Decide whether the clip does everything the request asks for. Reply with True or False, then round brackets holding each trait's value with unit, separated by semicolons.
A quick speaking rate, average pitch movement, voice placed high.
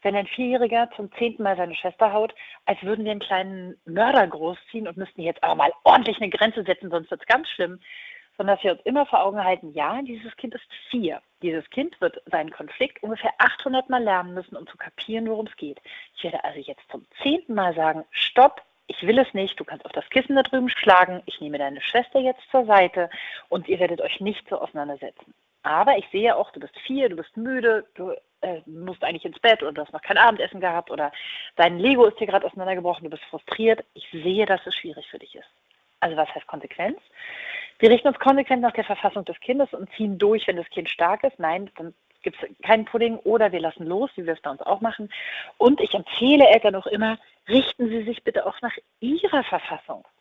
False (225 wpm; 5.7 semitones; 215 Hz)